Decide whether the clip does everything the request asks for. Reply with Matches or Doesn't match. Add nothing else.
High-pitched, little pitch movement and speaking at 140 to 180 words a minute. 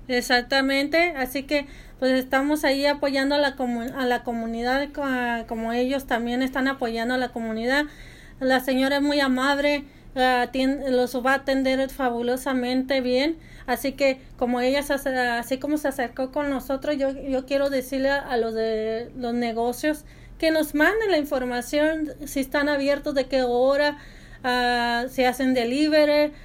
Matches